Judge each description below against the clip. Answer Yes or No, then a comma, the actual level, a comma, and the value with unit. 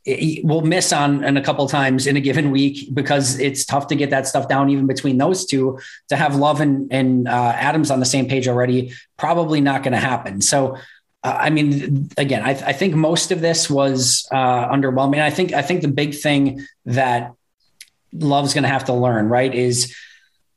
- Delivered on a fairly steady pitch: Yes, narrow, 1.9 semitones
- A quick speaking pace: Yes, fast, 215 wpm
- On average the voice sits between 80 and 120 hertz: No, medium, 140 Hz